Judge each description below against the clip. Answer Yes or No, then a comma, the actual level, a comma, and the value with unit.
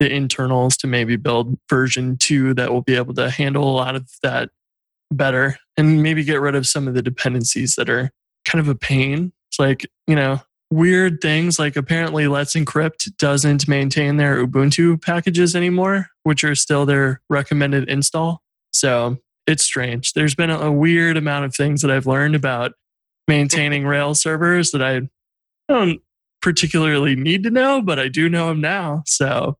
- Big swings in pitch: No, average, 3.3 semitones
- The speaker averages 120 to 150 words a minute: No, average, 175 wpm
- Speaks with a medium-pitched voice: Yes, medium, 145 Hz